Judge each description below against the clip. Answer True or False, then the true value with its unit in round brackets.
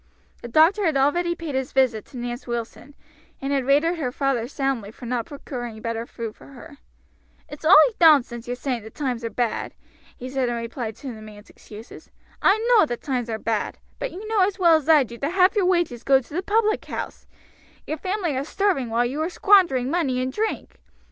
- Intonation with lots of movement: True (5.8 semitones)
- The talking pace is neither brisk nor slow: False (210 wpm)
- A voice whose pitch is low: False (270 Hz)